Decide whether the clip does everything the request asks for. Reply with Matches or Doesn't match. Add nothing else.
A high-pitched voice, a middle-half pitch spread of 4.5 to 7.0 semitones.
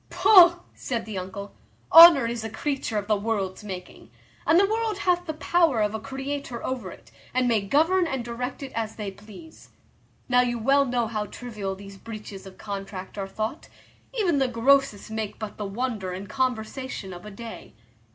Matches